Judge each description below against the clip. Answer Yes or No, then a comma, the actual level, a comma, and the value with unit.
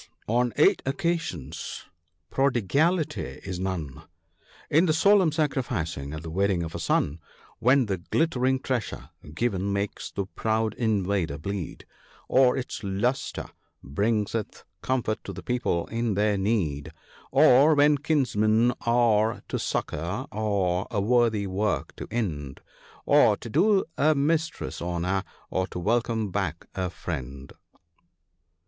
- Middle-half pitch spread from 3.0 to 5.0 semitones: No, wide, 5.6 semitones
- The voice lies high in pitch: No, low, 105 Hz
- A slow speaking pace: Yes, slow, 130 wpm